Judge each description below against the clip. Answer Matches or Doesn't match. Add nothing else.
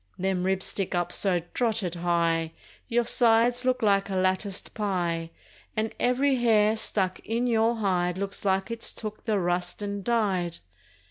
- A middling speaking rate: Matches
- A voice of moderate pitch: Doesn't match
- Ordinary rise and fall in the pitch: Matches